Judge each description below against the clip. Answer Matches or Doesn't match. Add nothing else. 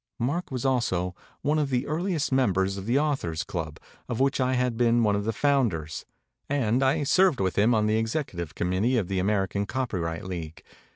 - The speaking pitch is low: Matches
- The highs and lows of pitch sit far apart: Matches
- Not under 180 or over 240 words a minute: Matches